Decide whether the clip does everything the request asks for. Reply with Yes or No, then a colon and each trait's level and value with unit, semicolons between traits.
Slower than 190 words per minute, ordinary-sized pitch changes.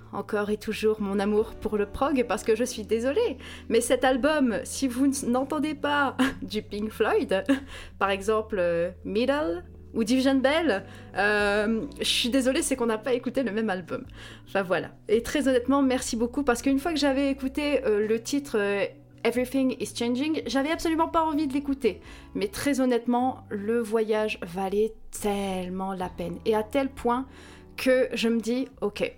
Yes: average, 175 wpm; average, 4.2 semitones